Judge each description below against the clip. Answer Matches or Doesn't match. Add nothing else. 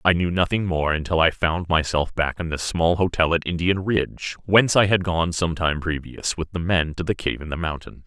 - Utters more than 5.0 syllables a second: Matches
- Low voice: Matches